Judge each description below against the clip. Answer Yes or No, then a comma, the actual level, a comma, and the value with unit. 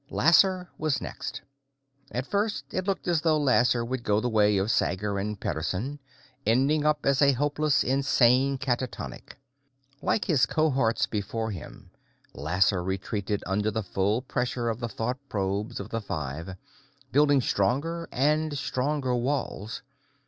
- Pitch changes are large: Yes, wide, 5.8 semitones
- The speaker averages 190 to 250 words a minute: No, average, 140 wpm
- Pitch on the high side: No, low, 125 Hz